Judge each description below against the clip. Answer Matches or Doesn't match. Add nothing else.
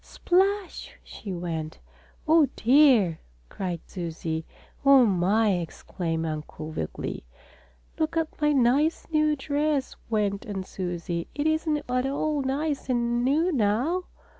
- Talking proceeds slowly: Matches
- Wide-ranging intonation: Matches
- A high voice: Matches